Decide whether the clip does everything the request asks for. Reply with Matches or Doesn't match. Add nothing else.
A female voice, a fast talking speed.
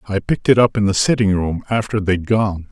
Doesn't match